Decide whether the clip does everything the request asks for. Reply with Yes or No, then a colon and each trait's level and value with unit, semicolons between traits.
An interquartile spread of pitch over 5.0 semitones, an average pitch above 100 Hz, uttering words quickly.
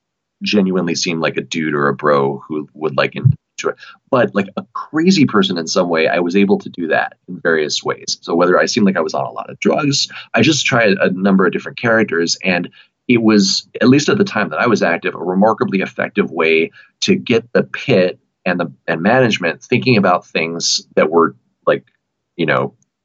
No: wide, 5.4 semitones; very low, 95 Hz; fast, 210 wpm